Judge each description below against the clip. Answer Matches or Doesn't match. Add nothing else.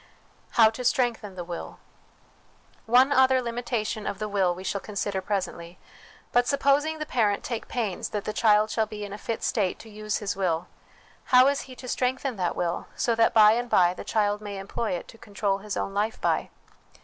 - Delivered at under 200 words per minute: Doesn't match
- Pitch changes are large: Doesn't match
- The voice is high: Matches